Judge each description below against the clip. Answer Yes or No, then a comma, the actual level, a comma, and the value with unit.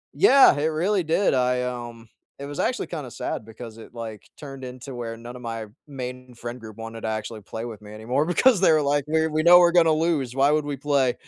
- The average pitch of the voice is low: Yes, low, 130 Hz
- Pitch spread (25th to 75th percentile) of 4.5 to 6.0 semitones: Yes, average, 5.0 semitones